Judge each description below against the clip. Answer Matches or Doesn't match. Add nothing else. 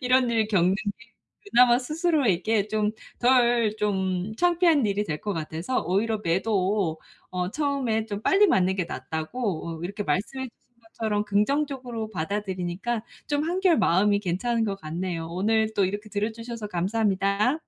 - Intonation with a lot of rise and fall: Doesn't match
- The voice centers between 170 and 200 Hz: Doesn't match